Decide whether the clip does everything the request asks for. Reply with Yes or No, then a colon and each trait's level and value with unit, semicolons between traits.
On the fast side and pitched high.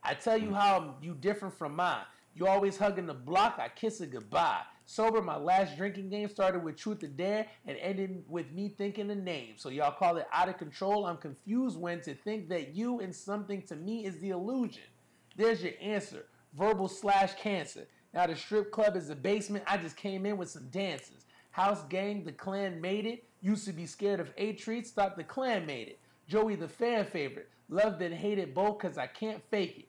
Yes: fast, 215 wpm; high, 195 Hz